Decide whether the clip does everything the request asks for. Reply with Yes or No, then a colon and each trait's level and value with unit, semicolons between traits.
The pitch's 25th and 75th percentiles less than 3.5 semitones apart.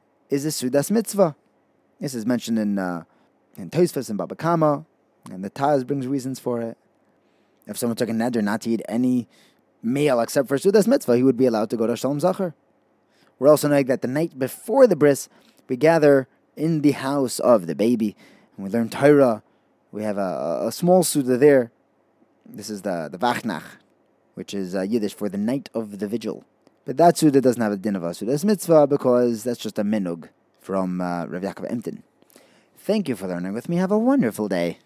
No: wide, 5.5 semitones